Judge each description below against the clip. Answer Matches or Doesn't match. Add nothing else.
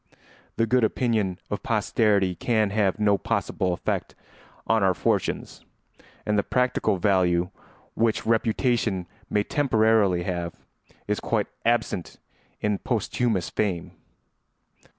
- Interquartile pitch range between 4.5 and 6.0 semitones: Doesn't match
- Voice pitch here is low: Matches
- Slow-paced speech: Matches